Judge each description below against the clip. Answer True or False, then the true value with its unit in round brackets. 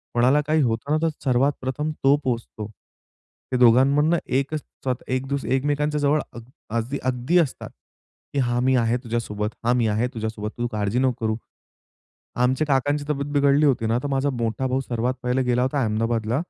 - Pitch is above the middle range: False (130 Hz)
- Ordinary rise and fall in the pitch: True (3.3 semitones)